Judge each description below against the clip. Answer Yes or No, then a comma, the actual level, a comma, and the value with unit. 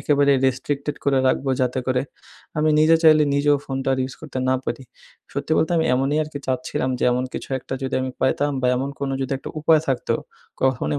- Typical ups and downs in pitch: No, narrow, 2.1 semitones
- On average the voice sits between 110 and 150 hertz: Yes, low, 135 Hz